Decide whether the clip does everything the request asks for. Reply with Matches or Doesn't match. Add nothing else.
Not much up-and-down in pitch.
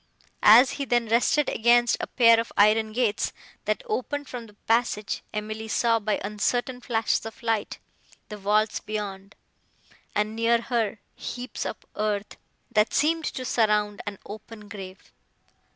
Matches